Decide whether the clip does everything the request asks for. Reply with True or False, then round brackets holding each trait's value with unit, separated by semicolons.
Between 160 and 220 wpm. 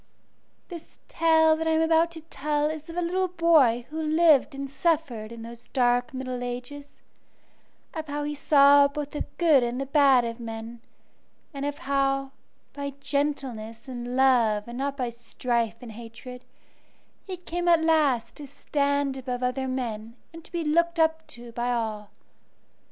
True (170 wpm)